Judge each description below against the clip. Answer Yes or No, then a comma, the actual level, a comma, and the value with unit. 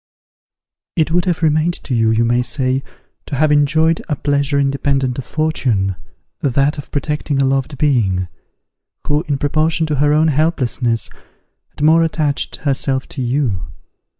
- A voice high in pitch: No, medium, 140 Hz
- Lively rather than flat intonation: No, average, 3.1 semitones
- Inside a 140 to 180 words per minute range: Yes, average, 150 wpm